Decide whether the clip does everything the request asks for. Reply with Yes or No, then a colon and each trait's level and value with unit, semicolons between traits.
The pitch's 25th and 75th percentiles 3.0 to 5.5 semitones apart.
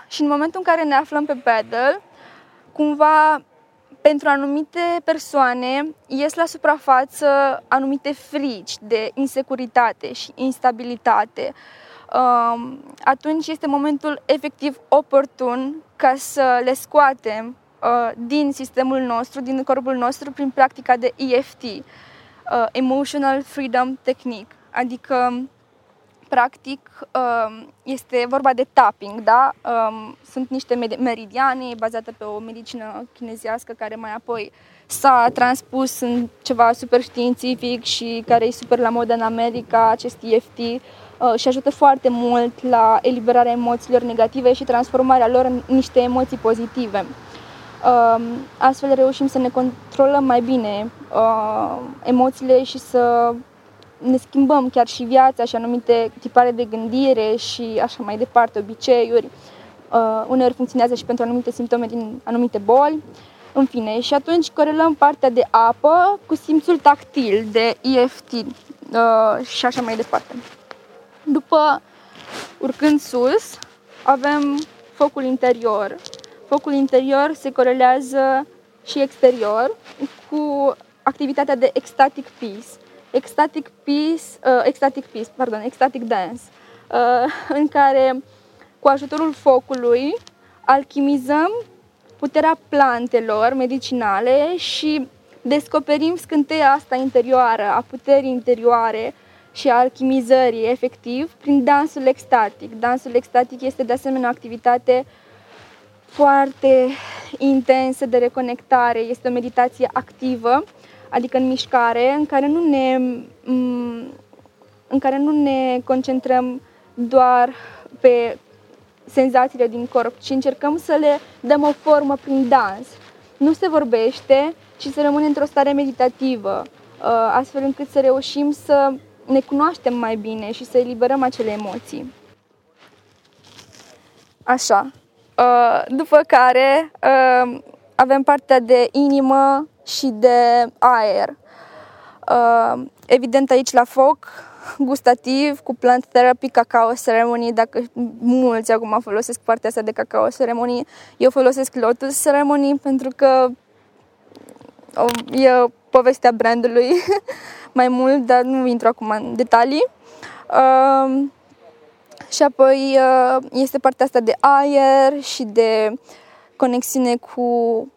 No: narrow, 2.4 semitones